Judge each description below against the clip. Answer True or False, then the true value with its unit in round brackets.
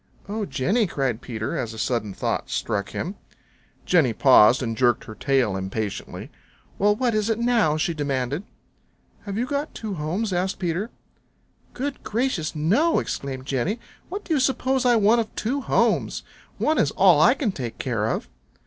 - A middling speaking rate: True (170 wpm)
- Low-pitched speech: False (175 Hz)